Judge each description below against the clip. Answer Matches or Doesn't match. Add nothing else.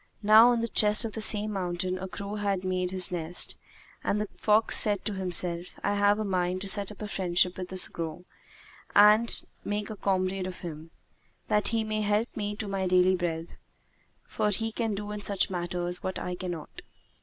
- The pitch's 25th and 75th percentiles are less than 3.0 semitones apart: Matches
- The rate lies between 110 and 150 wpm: Doesn't match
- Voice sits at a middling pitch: Doesn't match